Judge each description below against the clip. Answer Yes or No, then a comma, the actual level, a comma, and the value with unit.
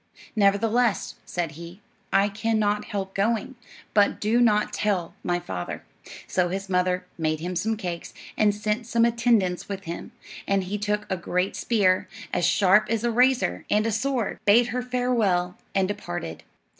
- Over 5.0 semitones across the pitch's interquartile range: No, average, 3.7 semitones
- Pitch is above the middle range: Yes, high, 205 Hz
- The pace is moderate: Yes, average, 165 wpm